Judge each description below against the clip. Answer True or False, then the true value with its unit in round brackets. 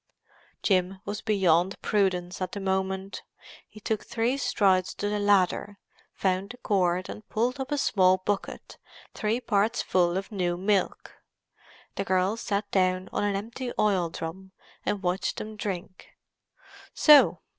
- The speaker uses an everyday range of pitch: False (2.3 semitones)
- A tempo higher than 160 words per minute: False (145 wpm)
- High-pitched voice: True (195 Hz)